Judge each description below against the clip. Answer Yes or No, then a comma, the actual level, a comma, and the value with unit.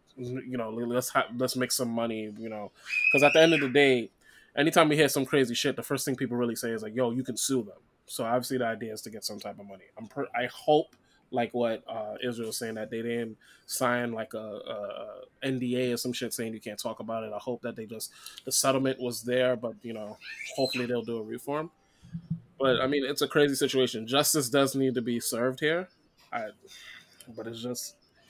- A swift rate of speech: Yes, fast, 230 wpm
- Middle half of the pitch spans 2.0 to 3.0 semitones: Yes, average, 2.7 semitones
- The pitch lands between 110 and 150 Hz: Yes, low, 125 Hz